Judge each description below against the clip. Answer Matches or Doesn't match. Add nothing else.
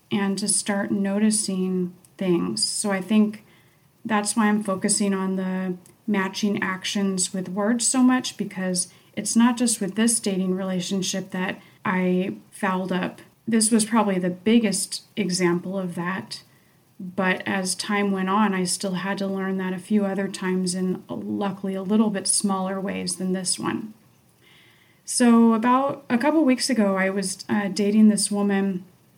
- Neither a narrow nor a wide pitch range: Doesn't match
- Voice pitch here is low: Doesn't match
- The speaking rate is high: Doesn't match